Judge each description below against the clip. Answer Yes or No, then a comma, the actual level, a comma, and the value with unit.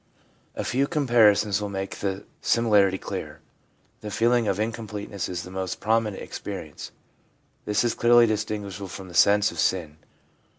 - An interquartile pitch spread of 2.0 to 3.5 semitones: Yes, average, 2.8 semitones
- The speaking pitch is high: No, low, 105 Hz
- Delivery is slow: No, average, 155 wpm